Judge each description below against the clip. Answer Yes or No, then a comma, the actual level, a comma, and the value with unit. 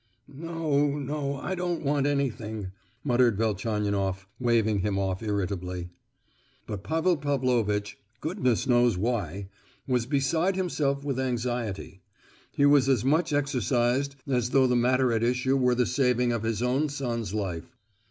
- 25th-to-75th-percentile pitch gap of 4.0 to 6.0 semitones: Yes, average, 4.7 semitones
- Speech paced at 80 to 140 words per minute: Yes, slow, 135 wpm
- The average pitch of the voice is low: Yes, low, 125 Hz